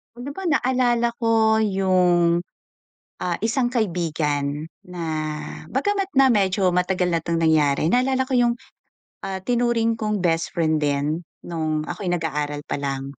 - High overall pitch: No, medium, 180 Hz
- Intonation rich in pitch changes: Yes, wide, 6.9 semitones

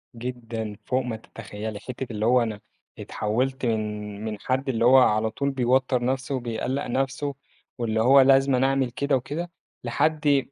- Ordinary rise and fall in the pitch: Yes, average, 3.3 semitones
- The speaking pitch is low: Yes, low, 125 Hz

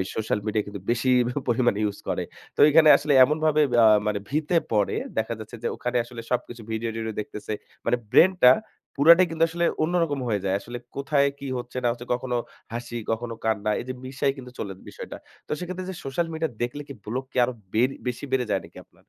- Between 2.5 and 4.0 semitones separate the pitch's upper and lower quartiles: No, average, 4.6 semitones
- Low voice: Yes, low, 125 Hz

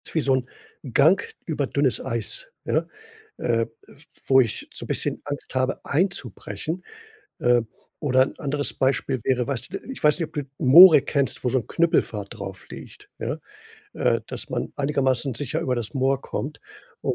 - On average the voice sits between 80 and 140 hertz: Yes, low, 135 Hz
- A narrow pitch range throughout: No, average, 3.3 semitones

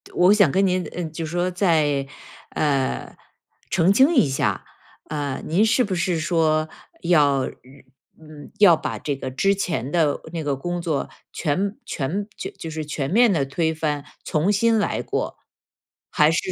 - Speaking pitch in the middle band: Yes, medium, 160 Hz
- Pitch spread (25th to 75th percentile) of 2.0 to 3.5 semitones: No, average, 4.2 semitones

